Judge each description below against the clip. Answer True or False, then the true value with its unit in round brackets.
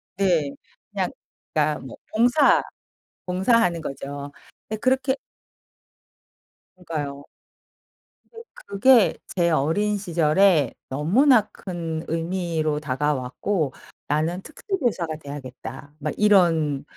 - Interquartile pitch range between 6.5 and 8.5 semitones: False (5.5 semitones)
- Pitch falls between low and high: True (165 Hz)